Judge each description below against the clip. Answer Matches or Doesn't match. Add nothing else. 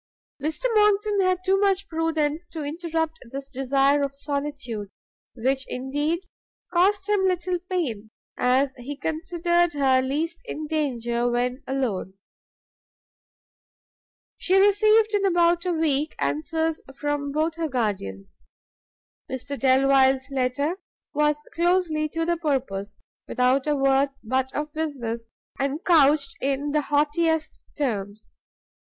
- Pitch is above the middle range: Matches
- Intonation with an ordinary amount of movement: Matches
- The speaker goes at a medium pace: Doesn't match